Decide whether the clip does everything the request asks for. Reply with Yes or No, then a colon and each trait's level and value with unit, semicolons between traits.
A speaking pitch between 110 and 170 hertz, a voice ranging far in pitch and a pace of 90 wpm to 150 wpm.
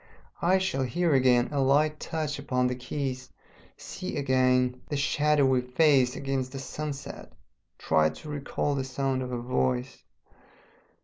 No: low, 135 Hz; narrow, 2.5 semitones; average, 140 wpm